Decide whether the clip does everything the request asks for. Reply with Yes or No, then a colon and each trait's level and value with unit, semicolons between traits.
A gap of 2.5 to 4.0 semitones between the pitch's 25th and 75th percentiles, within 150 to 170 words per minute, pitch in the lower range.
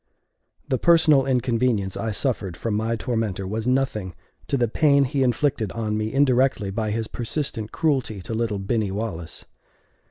Yes: average, 3.7 semitones; average, 155 wpm; low, 115 Hz